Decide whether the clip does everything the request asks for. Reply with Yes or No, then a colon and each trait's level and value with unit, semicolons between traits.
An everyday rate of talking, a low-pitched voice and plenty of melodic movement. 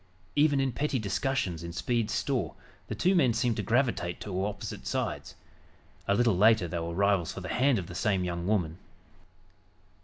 Yes: average, 180 wpm; low, 105 Hz; wide, 5.7 semitones